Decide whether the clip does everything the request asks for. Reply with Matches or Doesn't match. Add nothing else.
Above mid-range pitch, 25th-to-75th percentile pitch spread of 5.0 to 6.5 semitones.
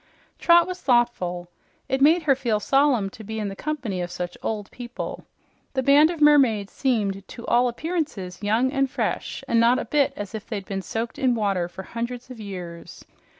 Matches